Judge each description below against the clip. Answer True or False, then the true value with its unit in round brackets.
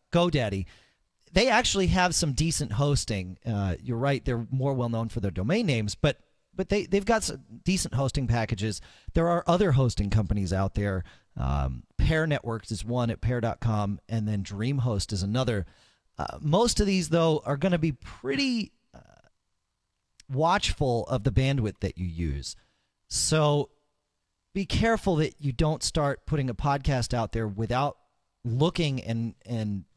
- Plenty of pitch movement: True (6.8 semitones)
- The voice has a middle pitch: False (125 Hz)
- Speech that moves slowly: False (160 wpm)